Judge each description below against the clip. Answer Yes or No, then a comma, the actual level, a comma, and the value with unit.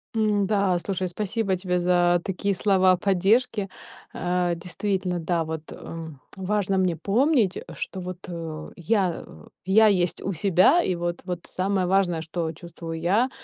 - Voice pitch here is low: No, medium, 185 Hz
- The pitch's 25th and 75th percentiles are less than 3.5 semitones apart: Yes, narrow, 2.4 semitones